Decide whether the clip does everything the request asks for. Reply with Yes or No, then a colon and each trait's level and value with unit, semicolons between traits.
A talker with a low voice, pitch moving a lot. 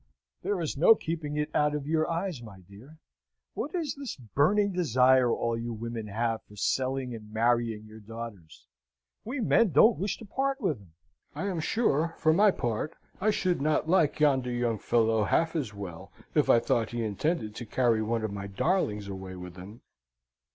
Yes: low, 125 Hz; wide, 7.2 semitones